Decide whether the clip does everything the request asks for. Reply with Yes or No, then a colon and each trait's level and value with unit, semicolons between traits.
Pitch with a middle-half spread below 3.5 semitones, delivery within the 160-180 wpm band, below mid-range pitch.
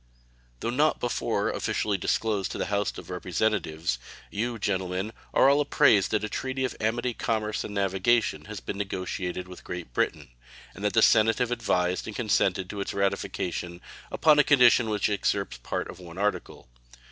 No: average, 4.0 semitones; average, 170 wpm; low, 105 Hz